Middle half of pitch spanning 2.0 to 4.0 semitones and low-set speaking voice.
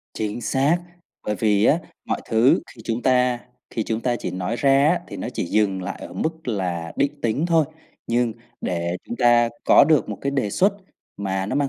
No: average, 5.3 semitones; low, 115 Hz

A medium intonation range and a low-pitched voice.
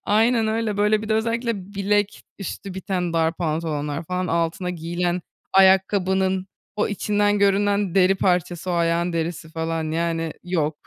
No: average, 3.5 semitones; medium, 185 Hz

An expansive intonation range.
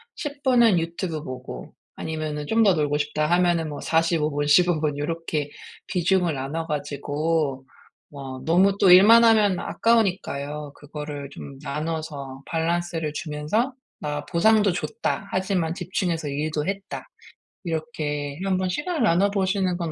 No: average, 4.1 semitones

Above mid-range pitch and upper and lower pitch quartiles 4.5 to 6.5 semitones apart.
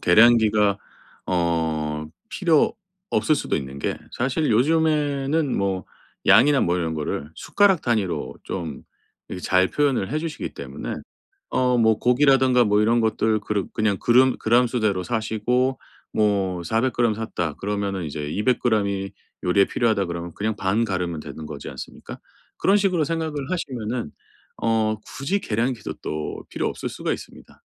No: low, 110 Hz; wide, 5.4 semitones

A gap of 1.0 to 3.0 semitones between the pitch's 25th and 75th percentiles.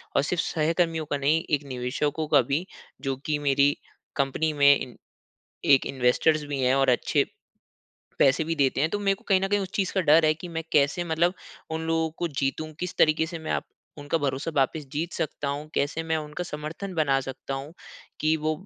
Yes: average, 2.7 semitones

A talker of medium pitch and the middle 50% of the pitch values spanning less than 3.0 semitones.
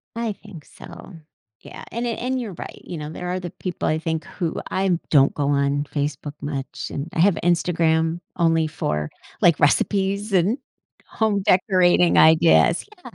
No: medium, 170 Hz; average, 3.8 semitones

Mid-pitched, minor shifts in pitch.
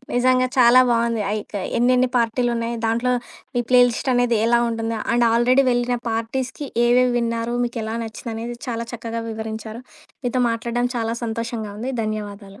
No: high, 235 Hz; narrow, 1.4 semitones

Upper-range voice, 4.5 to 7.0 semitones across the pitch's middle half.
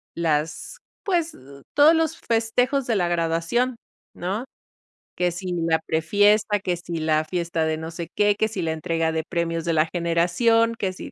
No: medium, 175 Hz; average, 5.2 semitones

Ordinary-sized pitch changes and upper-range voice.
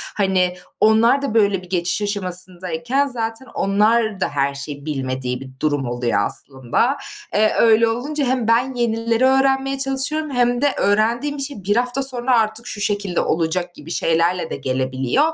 No: wide, 6.4 semitones; high, 215 Hz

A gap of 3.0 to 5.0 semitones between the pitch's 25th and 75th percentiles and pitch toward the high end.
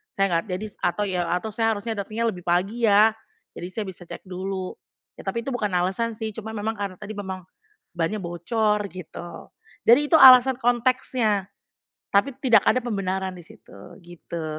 Yes: average, 3.7 semitones; high, 205 Hz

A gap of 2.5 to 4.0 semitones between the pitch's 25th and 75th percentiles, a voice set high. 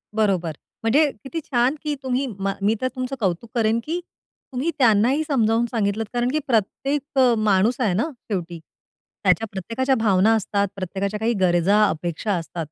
No: average, 4.7 semitones; high, 225 Hz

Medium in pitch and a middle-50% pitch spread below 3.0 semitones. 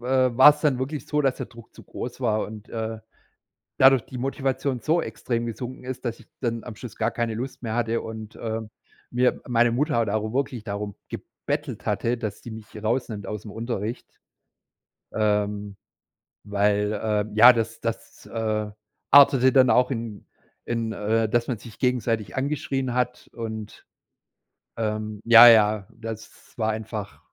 No: low, 115 Hz; narrow, 2.6 semitones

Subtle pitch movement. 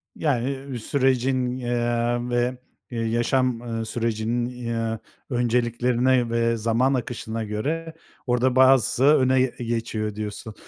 Yes: narrow, 2.1 semitones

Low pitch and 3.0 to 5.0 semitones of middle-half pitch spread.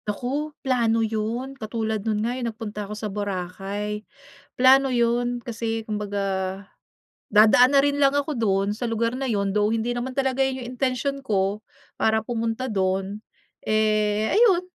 No: high, 225 Hz; average, 3.3 semitones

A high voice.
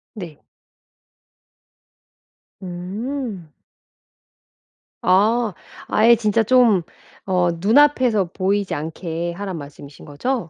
Yes: high, 195 Hz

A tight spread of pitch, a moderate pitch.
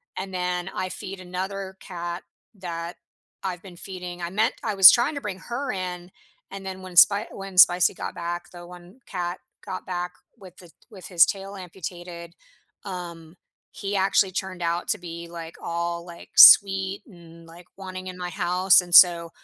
Yes: narrow, 1.8 semitones; medium, 180 Hz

